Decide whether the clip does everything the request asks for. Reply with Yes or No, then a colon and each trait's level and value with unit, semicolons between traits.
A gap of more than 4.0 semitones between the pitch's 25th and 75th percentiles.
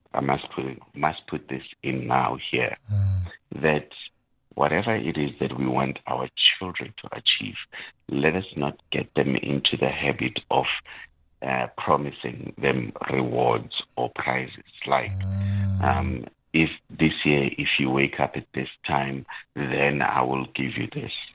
No: average, 3.4 semitones